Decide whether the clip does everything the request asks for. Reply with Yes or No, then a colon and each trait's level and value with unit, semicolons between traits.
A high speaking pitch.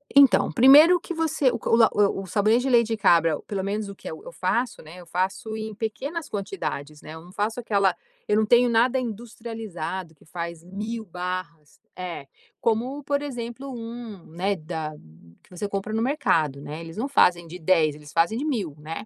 Yes: high, 205 Hz